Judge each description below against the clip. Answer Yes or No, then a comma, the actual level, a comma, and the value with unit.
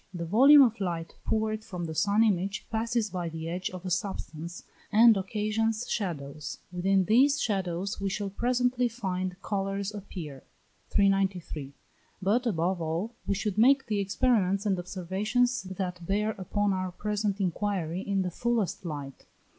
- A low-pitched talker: No, high, 195 Hz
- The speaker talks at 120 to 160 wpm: Yes, average, 150 wpm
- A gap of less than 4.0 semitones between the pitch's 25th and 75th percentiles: Yes, average, 3.3 semitones